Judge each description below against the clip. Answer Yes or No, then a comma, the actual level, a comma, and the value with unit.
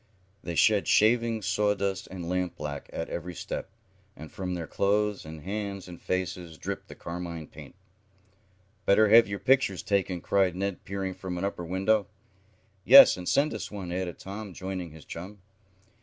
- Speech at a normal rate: Yes, average, 160 wpm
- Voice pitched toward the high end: No, very low, 95 Hz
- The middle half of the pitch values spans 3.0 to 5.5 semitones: No, narrow, 2.4 semitones